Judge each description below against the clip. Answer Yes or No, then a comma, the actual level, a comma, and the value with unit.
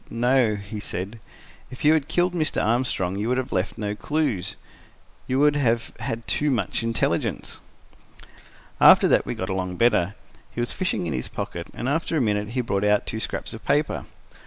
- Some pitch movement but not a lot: Yes, average, 4.7 semitones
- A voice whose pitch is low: Yes, low, 115 Hz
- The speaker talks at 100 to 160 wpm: No, average, 185 wpm